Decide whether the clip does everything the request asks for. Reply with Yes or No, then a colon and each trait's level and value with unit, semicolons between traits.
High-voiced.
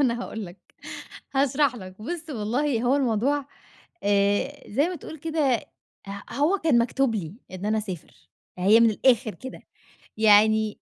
Yes: high, 235 Hz